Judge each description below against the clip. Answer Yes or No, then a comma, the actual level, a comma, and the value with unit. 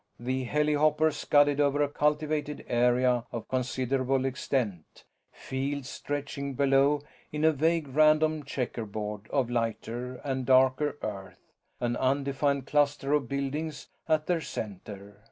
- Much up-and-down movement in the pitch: No, average, 3.1 semitones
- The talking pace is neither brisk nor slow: No, slow, 120 wpm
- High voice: No, low, 135 Hz